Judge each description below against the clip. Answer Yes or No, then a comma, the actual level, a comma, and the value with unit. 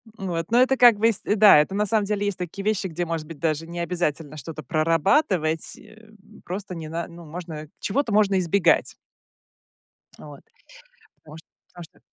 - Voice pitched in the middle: Yes, medium, 175 Hz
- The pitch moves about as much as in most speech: Yes, average, 4.2 semitones